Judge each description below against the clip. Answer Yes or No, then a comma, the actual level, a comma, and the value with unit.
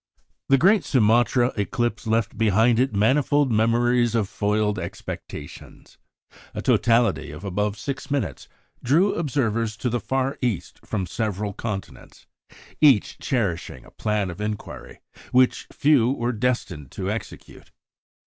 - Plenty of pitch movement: No, average, 3.5 semitones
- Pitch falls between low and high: No, low, 115 Hz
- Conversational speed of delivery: No, slow, 130 wpm